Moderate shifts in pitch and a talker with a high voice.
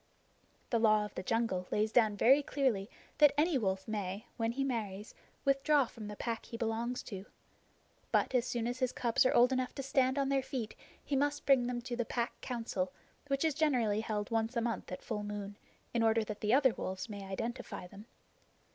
Yes: average, 3.8 semitones; high, 230 Hz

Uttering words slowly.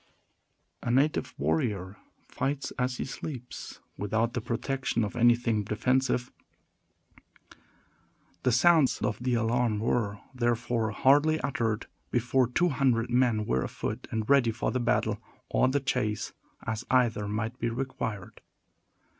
Yes: slow, 130 wpm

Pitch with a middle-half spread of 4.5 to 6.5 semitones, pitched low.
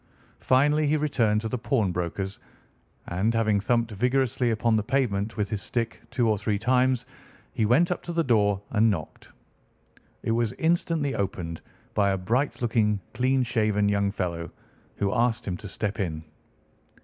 No: average, 3.9 semitones; low, 110 Hz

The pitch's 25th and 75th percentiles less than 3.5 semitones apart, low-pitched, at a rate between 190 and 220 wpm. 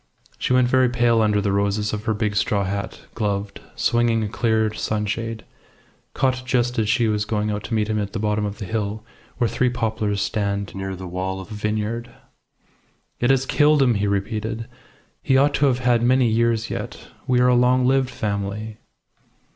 Yes: average, 2.9 semitones; low, 110 Hz; average, 195 wpm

